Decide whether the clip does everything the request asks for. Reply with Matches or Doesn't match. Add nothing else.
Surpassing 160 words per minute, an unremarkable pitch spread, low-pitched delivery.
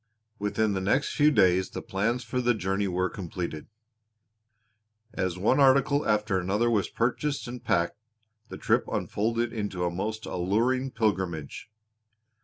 Doesn't match